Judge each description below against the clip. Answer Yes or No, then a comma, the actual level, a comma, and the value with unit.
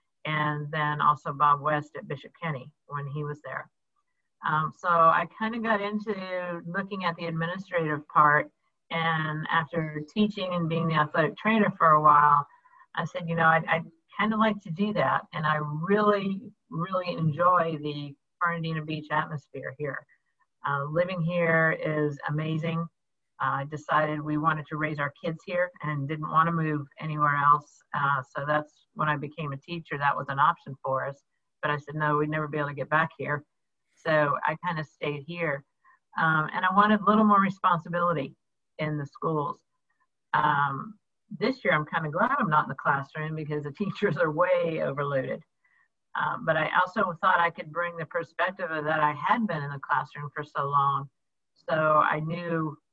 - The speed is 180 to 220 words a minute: Yes, average, 185 wpm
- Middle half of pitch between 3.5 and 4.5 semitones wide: No, average, 2.8 semitones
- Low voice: No, medium, 155 Hz